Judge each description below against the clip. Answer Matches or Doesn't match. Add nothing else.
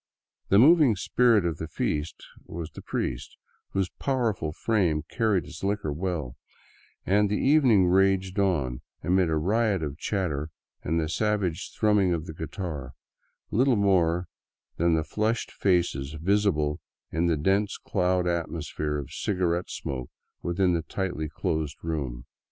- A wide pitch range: Doesn't match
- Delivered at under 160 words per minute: Matches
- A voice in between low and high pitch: Doesn't match